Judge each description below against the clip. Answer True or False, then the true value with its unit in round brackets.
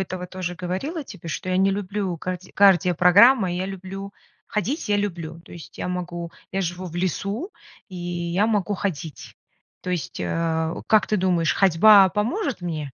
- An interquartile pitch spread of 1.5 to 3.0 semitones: True (2.6 semitones)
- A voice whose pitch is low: False (185 Hz)